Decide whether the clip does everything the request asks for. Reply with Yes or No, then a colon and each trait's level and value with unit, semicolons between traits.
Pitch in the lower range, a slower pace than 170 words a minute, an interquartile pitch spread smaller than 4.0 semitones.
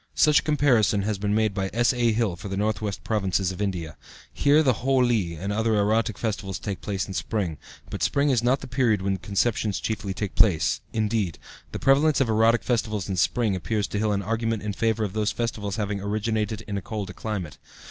No: low, 105 Hz; fast, 205 wpm; narrow, 2.6 semitones